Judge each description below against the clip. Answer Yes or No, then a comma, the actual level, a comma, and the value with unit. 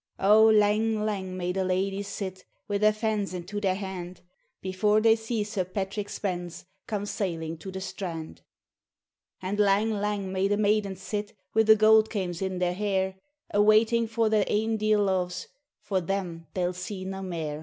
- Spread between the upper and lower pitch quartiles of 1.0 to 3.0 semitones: Yes, narrow, 2.4 semitones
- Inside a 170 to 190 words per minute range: Yes, average, 175 wpm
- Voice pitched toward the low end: No, high, 200 Hz